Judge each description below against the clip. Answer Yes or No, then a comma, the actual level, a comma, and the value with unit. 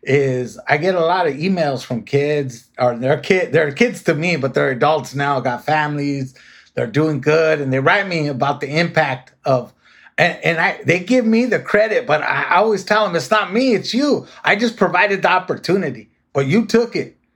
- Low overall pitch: No, medium, 155 Hz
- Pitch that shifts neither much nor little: No, wide, 6.3 semitones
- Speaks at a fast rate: Yes, fast, 210 wpm